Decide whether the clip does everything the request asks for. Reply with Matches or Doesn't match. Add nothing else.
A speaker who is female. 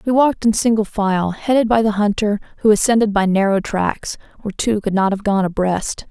Matches